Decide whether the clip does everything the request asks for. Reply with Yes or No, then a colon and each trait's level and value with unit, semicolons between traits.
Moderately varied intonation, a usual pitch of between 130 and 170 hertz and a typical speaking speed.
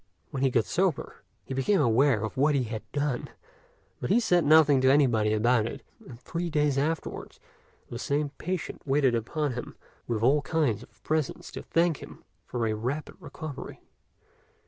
Yes: average, 4.3 semitones; low, 135 Hz; average, 170 wpm